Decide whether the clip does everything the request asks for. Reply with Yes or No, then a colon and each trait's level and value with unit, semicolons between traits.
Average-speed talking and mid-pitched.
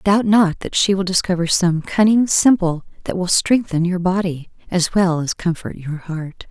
Yes: average, 185 wpm; medium, 180 Hz